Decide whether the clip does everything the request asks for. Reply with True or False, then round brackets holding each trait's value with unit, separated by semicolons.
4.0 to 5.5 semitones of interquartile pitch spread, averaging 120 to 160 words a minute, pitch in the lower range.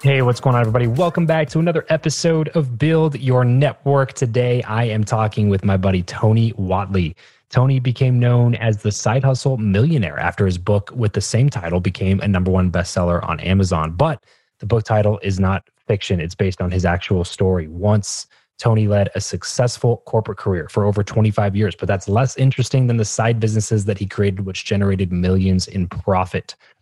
False (4.5 semitones; 190 wpm; 105 Hz)